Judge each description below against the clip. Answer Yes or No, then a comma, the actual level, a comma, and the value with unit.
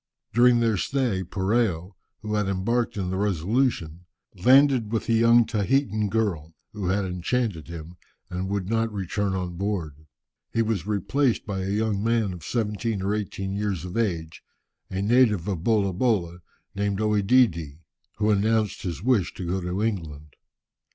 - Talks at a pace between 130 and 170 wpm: Yes, average, 155 wpm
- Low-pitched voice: Yes, low, 100 Hz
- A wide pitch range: No, average, 3.8 semitones